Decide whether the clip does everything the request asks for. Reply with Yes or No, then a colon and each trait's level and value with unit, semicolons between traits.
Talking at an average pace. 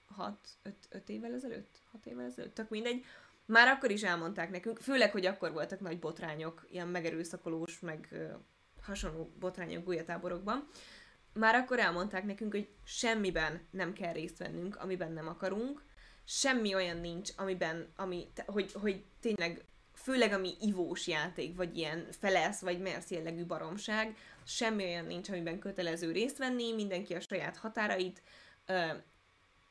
Yes: average, 145 wpm